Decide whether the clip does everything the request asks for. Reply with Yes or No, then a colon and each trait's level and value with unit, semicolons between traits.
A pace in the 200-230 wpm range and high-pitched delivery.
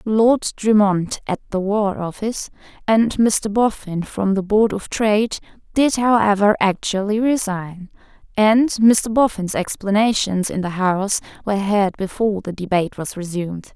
No: average, 140 wpm; high, 205 Hz